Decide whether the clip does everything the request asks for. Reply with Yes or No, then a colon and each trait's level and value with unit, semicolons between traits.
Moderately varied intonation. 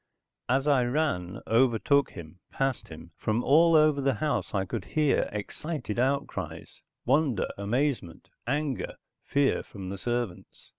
No: wide, 5.8 semitones